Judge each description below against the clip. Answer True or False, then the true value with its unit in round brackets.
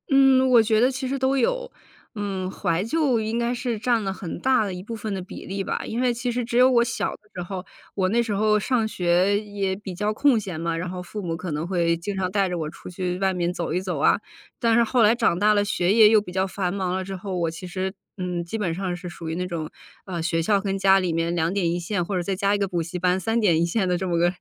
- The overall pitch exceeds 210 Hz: False (195 Hz)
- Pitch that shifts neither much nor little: True (3.8 semitones)